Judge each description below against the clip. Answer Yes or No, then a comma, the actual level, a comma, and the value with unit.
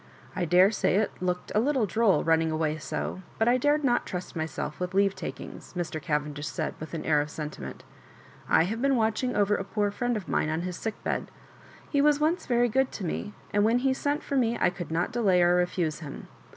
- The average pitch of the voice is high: Yes, high, 195 Hz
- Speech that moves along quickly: Yes, fast, 215 wpm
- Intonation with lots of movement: Yes, wide, 6.6 semitones